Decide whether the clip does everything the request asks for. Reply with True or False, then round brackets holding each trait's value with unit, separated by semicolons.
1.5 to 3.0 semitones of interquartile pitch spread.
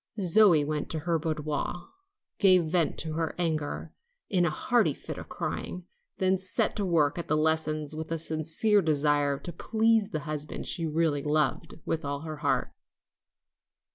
True (2.7 semitones)